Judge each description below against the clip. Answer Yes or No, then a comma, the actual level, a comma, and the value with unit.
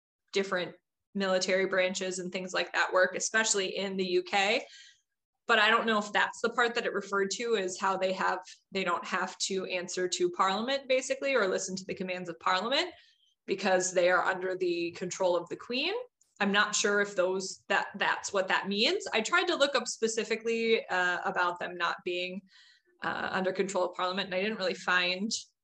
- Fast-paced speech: No, average, 195 wpm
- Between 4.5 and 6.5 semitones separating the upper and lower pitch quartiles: No, average, 3.4 semitones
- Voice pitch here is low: No, high, 195 Hz